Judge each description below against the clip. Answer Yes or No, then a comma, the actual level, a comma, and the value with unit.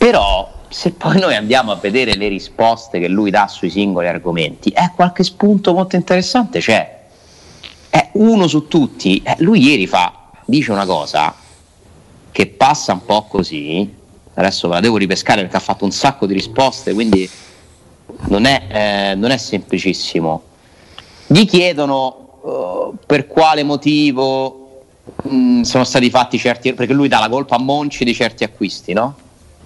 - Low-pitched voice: Yes, low, 120 Hz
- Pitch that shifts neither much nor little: No, wide, 7.5 semitones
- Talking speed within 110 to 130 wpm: No, average, 160 wpm